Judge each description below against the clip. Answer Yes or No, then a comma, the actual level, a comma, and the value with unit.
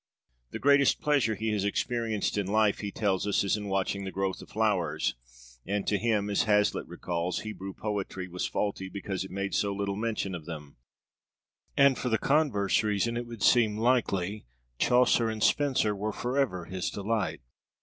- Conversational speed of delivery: Yes, average, 175 wpm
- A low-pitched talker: Yes, low, 105 Hz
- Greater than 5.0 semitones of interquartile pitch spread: No, average, 2.8 semitones